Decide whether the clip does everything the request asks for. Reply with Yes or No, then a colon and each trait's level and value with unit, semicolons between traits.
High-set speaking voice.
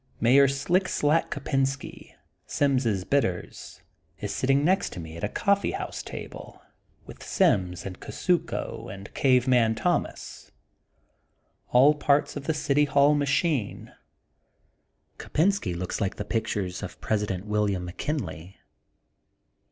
No: low, 130 Hz